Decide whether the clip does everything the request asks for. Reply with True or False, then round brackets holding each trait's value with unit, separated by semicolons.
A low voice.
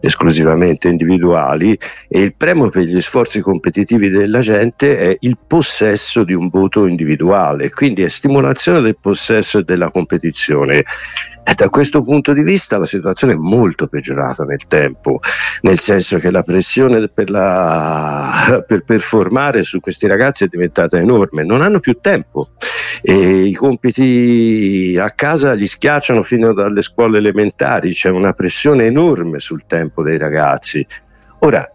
True (100 Hz)